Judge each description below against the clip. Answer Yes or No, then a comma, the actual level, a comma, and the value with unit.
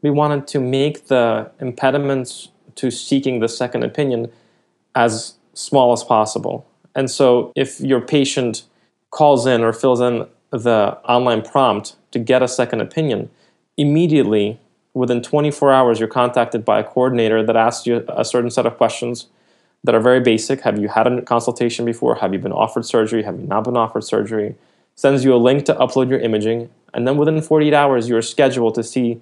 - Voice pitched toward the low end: Yes, low, 125 Hz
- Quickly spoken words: No, average, 180 wpm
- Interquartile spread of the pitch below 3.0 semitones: Yes, narrow, 2.6 semitones